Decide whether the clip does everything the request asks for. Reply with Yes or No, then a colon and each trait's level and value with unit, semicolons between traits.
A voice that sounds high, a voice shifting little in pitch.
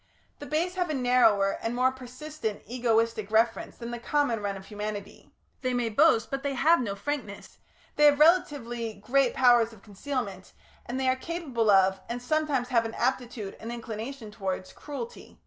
No: high, 240 Hz; average, 4.0 semitones